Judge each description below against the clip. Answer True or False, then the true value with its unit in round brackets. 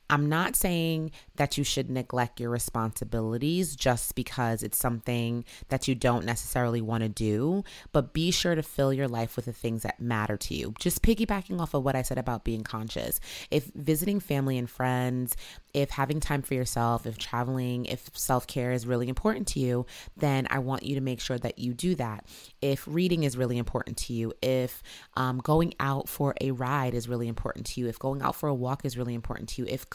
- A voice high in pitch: False (125 Hz)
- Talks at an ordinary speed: False (210 wpm)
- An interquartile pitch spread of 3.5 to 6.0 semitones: False (3.1 semitones)